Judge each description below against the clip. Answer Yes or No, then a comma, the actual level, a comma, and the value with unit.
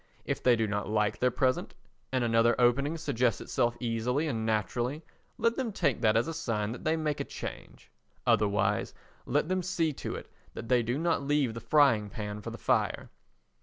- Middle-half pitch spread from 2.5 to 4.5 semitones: No, average, 5.0 semitones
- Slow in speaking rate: No, average, 195 wpm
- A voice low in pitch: Yes, low, 120 Hz